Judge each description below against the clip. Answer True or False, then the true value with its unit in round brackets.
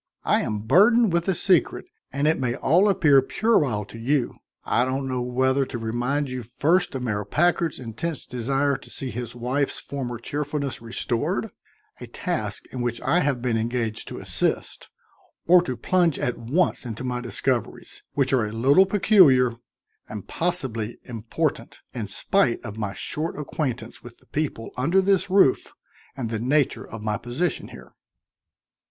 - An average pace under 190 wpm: True (165 wpm)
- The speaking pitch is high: False (130 Hz)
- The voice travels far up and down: False (4.8 semitones)